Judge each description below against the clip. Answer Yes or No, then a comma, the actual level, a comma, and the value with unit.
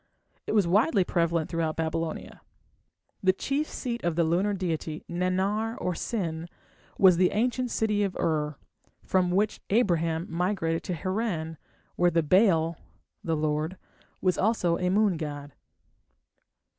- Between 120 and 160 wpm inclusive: Yes, slow, 135 wpm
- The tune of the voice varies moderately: Yes, average, 3.7 semitones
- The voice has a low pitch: No, medium, 180 Hz